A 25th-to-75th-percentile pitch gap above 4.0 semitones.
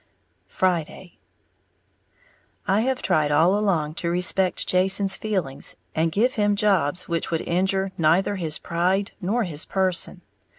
No: average, 2.9 semitones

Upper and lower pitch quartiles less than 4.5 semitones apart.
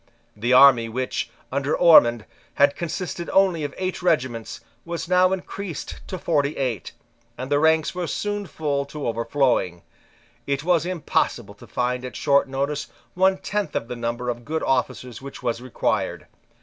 No: wide, 5.4 semitones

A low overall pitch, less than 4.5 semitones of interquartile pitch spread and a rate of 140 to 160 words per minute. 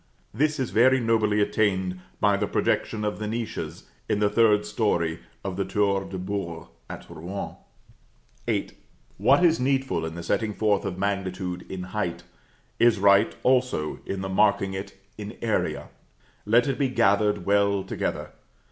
Yes: low, 100 Hz; average, 2.7 semitones; average, 155 wpm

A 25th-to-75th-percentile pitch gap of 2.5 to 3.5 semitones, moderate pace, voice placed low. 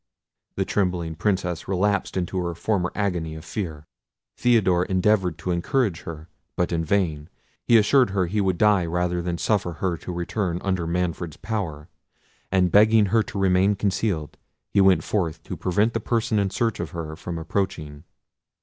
Yes: average, 3.2 semitones; average, 170 wpm; very low, 90 Hz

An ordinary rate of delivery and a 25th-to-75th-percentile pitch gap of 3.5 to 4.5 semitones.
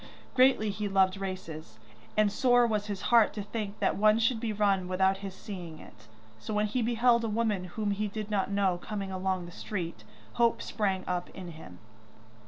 No: average, 190 wpm; narrow, 2.6 semitones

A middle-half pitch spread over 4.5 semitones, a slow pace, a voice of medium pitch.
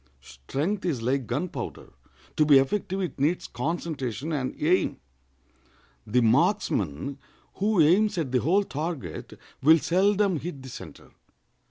Yes: wide, 5.5 semitones; slow, 130 wpm; medium, 150 Hz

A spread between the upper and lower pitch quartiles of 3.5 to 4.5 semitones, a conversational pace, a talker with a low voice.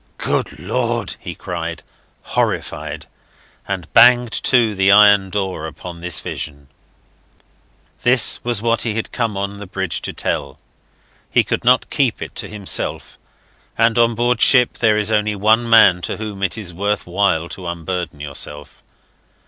Yes: average, 4.2 semitones; average, 155 wpm; low, 105 Hz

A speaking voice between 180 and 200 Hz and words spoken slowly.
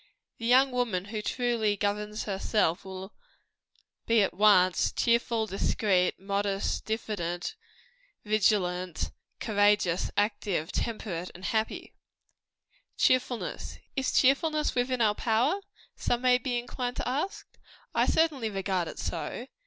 No: high, 215 Hz; slow, 115 wpm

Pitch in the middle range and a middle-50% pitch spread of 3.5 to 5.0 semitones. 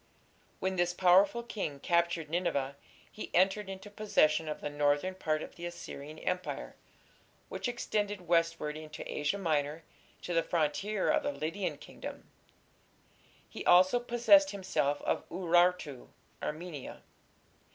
Yes: medium, 175 Hz; average, 3.9 semitones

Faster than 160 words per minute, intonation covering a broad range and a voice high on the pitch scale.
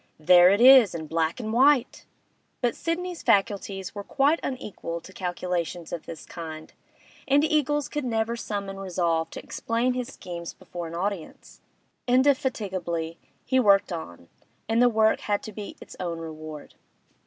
No: average, 155 wpm; wide, 6.7 semitones; high, 200 Hz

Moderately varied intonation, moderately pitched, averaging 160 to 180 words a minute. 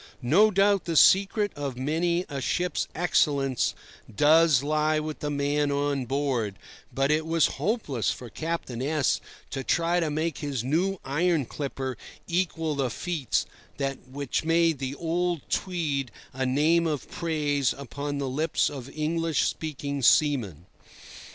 No: average, 3.3 semitones; medium, 150 Hz; average, 140 wpm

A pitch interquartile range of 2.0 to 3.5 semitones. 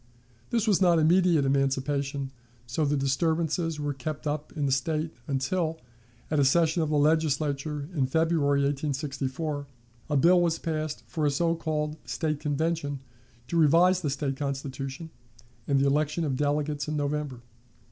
Yes: narrow, 2.5 semitones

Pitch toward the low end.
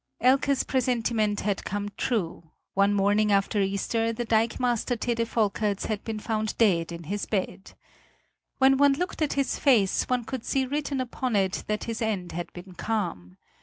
No: high, 220 Hz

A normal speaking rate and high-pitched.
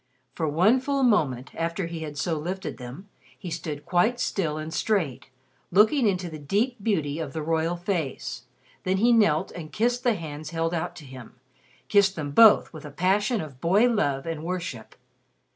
No: average, 180 wpm; medium, 170 Hz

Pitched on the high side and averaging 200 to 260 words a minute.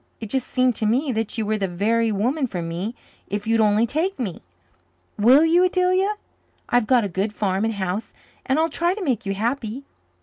Yes: high, 230 Hz; fast, 205 wpm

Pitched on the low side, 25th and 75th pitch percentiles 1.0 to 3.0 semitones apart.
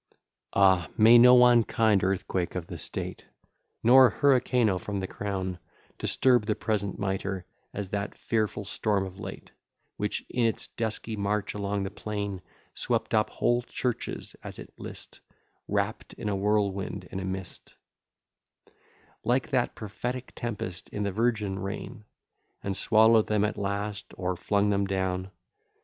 Yes: low, 105 Hz; average, 2.7 semitones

